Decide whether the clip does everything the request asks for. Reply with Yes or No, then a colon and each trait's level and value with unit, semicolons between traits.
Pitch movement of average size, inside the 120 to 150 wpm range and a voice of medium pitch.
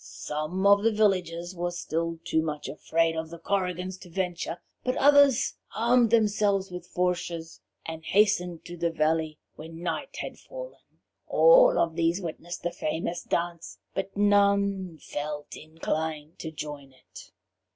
Yes: average, 3.7 semitones; average, 145 wpm; medium, 175 Hz